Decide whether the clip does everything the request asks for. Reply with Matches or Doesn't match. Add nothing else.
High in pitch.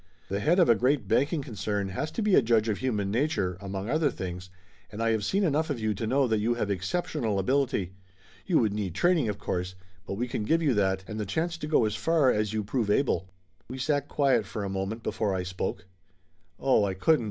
Doesn't match